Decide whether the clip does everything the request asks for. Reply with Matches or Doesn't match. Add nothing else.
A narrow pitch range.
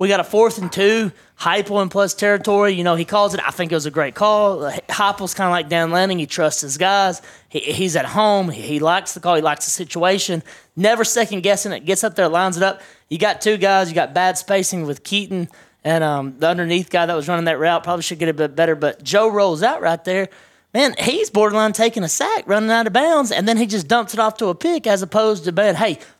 Doesn't match